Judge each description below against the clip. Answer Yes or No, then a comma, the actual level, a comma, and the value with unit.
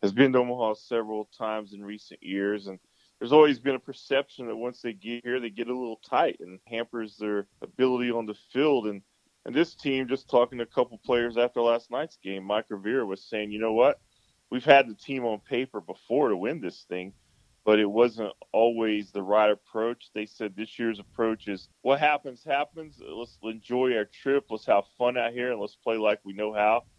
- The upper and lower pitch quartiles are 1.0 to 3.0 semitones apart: Yes, average, 2.7 semitones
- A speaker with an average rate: No, fast, 215 wpm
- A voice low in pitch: Yes, low, 115 Hz